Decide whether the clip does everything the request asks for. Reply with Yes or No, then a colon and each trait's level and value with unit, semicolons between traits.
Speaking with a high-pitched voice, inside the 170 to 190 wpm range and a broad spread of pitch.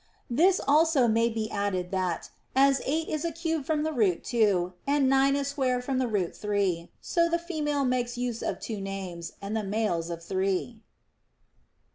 Yes: high, 240 Hz; average, 180 wpm; wide, 6.4 semitones